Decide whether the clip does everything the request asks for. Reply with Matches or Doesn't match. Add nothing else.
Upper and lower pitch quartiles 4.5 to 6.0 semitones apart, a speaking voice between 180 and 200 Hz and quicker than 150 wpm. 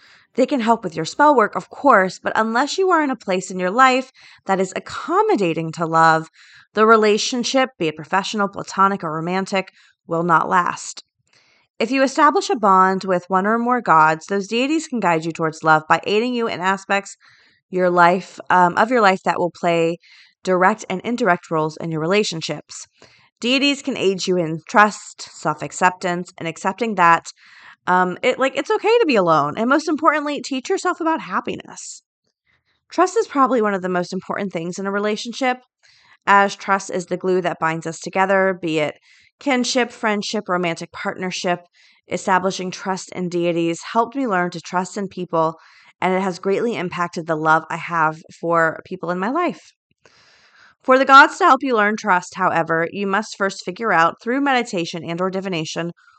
Matches